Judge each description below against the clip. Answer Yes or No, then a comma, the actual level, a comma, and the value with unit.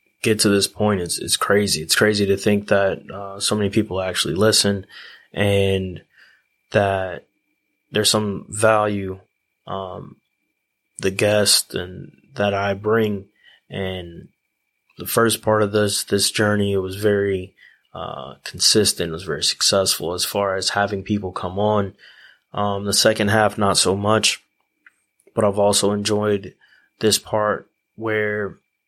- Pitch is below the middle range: Yes, low, 100 Hz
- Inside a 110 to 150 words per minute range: Yes, average, 140 wpm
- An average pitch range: No, narrow, 1.5 semitones